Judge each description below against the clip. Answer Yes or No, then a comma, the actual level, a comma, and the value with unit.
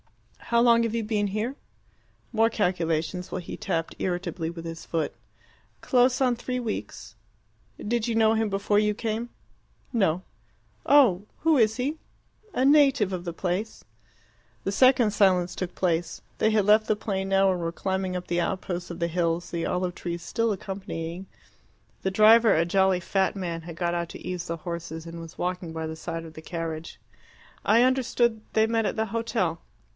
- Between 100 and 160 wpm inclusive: No, average, 180 wpm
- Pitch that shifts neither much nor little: Yes, average, 4.5 semitones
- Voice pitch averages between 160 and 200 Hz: Yes, high, 190 Hz